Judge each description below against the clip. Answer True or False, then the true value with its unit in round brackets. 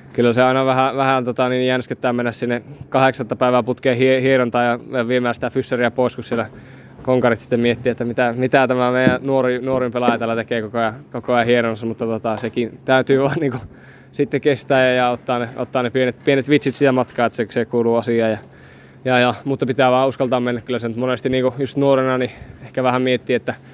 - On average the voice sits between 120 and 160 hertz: True (125 Hz)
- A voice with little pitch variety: True (1.5 semitones)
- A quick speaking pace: True (210 wpm)